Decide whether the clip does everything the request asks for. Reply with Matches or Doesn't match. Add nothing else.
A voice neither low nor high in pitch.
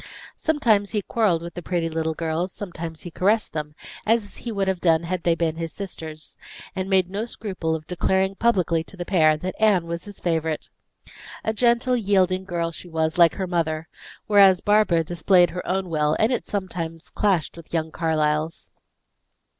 Matches